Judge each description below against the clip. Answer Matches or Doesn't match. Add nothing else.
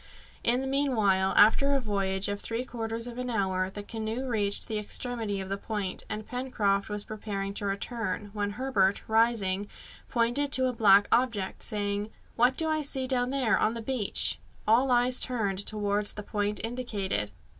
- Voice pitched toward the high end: Matches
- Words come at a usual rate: Matches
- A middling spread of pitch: Matches